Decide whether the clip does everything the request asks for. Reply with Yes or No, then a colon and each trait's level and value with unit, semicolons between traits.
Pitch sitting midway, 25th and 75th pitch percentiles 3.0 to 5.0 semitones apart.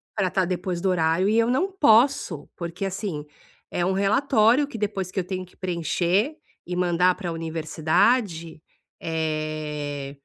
Yes: medium, 180 Hz; average, 4.2 semitones